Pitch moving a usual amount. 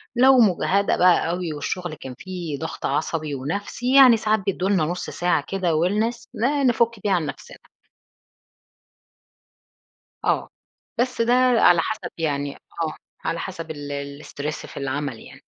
No: wide, 6.0 semitones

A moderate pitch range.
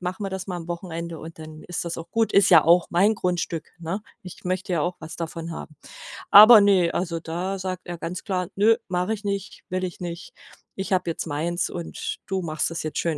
No: narrow, 2.3 semitones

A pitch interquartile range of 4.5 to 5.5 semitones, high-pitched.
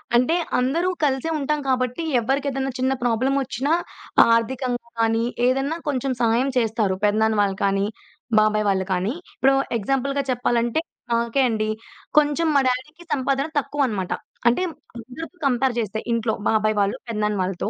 No: average, 3.8 semitones; high, 245 Hz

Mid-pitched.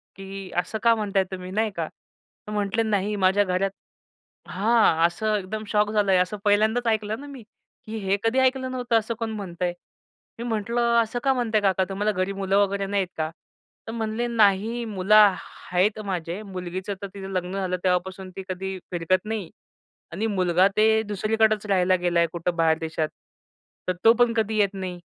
No: high, 200 Hz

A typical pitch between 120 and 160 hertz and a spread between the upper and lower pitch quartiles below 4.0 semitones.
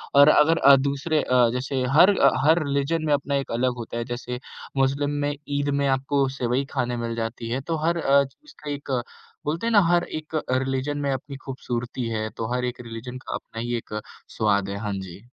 Yes: low, 135 Hz; average, 3.1 semitones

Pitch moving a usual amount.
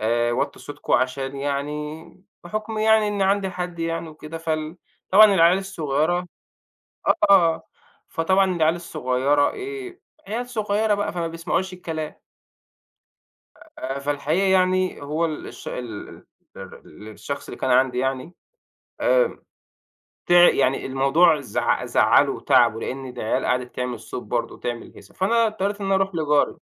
No: wide, 5.7 semitones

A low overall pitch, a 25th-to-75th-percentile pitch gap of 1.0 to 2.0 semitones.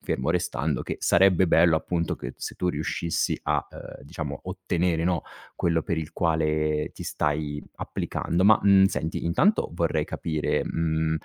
No: very low, 80 Hz; narrow, 2.4 semitones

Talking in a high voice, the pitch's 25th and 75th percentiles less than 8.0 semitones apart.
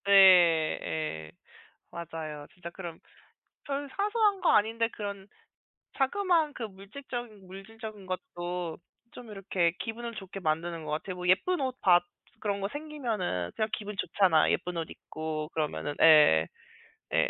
Yes: high, 195 Hz; wide, 5.4 semitones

